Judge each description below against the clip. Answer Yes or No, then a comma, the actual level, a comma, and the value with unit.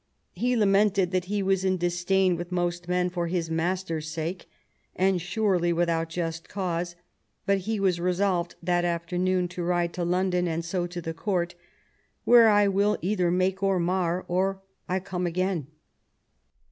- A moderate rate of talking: Yes, average, 170 wpm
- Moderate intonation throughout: No, narrow, 1.8 semitones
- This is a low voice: No, medium, 180 Hz